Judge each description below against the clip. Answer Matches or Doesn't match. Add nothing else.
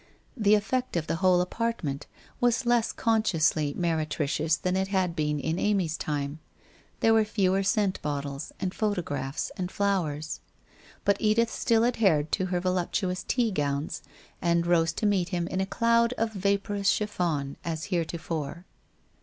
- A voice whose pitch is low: Doesn't match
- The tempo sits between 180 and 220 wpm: Doesn't match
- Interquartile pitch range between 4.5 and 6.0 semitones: Matches